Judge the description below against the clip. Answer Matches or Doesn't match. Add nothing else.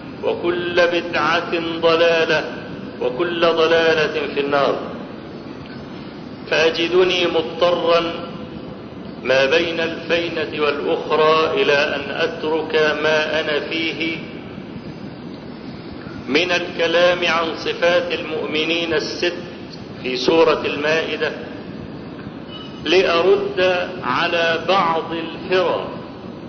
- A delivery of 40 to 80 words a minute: Matches